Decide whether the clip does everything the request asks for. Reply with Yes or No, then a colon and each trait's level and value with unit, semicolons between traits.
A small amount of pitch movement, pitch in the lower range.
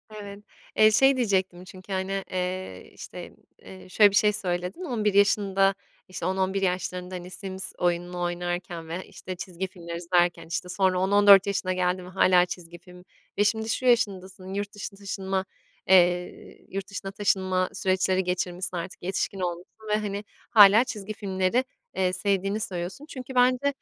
No: narrow, 1.9 semitones; high, 190 Hz